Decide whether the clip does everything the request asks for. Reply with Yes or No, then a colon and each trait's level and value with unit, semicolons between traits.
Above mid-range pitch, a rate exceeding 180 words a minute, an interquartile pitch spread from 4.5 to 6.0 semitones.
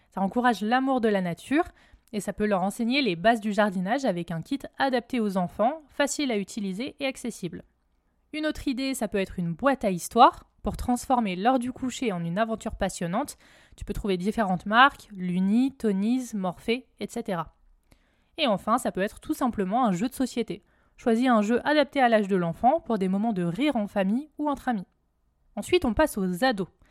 Yes: high, 225 Hz; average, 195 wpm; average, 4.9 semitones